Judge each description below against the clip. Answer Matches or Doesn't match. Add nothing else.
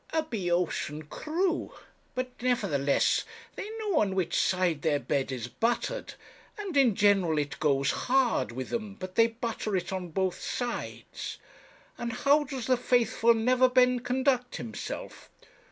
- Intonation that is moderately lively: Doesn't match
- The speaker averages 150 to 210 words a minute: Doesn't match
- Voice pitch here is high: Matches